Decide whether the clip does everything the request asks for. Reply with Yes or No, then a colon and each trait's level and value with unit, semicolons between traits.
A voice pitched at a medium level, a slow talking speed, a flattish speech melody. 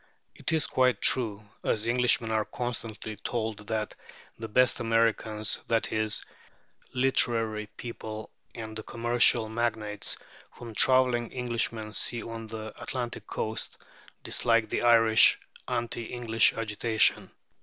No: low, 115 Hz; slow, 125 wpm; narrow, 1.5 semitones